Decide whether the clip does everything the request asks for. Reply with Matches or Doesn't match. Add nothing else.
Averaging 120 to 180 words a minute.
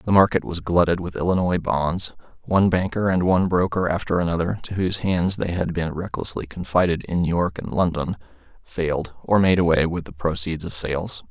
Doesn't match